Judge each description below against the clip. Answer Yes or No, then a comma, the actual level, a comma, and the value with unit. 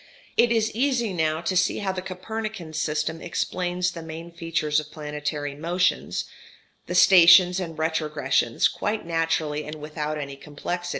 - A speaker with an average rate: Yes, average, 145 wpm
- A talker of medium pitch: Yes, medium, 165 Hz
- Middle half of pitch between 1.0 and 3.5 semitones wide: Yes, average, 3.1 semitones